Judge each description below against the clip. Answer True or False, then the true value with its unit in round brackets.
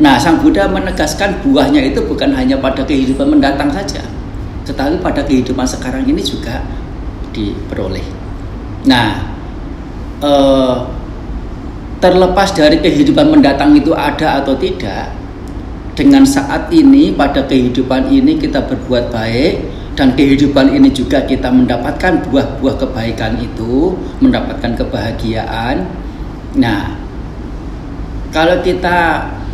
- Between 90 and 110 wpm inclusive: True (105 wpm)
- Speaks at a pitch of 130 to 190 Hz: True (140 Hz)